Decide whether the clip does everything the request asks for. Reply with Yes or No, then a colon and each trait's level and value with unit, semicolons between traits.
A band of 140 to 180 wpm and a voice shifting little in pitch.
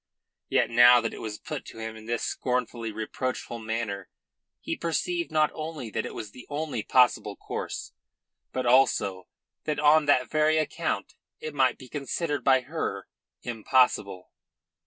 No: average, 155 wpm; average, 4.9 semitones